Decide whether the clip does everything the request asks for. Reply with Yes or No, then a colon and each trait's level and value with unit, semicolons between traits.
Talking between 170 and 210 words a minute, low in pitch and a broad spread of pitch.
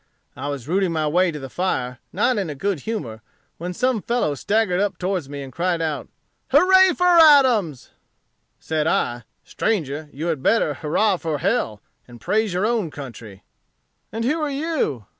No: average, 175 wpm; medium, 175 Hz; wide, 7.7 semitones